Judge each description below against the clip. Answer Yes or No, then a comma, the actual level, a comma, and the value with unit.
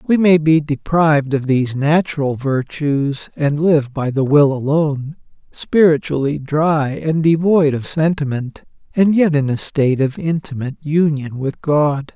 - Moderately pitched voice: Yes, medium, 150 Hz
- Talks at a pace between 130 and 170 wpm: Yes, average, 150 wpm